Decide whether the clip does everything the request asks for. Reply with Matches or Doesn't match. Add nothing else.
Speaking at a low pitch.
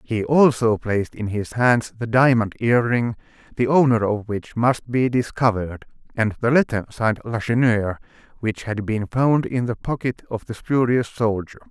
Matches